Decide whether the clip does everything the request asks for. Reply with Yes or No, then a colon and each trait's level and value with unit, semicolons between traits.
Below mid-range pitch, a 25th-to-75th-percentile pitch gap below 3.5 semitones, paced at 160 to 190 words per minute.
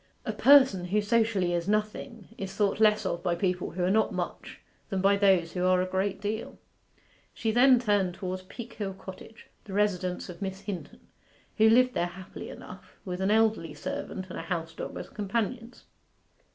No: high, 195 Hz; average, 3.1 semitones; average, 180 wpm